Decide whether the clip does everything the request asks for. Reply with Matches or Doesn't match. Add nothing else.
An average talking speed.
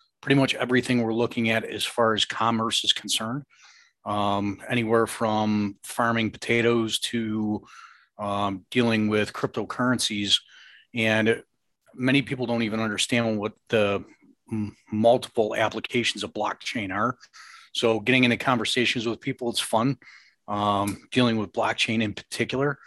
Doesn't match